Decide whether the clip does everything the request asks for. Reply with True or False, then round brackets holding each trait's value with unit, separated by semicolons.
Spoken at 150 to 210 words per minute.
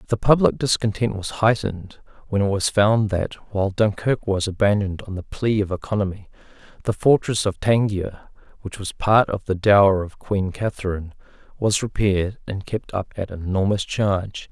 True (170 wpm)